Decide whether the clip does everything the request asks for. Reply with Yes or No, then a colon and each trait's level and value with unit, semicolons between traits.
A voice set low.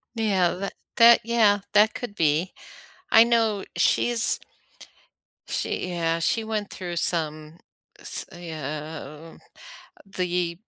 No: medium, 180 Hz